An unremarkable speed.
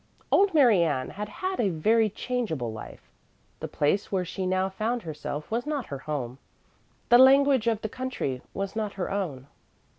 Yes: average, 175 wpm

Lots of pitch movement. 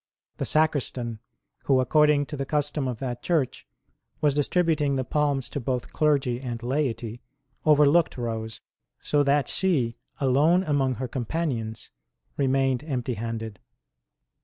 No: average, 3.5 semitones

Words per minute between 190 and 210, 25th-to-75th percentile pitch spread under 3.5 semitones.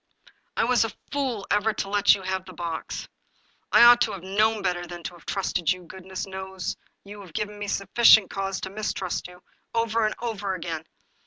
Yes: average, 200 wpm; average, 2.8 semitones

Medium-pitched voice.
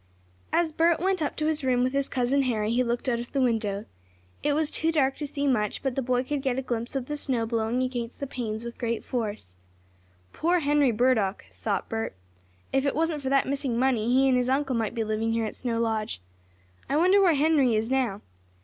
No: very high, 255 Hz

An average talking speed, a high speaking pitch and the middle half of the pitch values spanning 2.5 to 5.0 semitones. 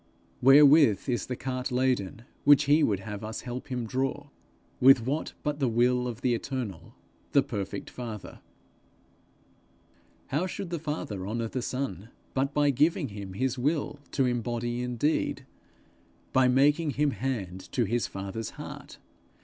No: average, 150 wpm; low, 125 Hz; average, 3.8 semitones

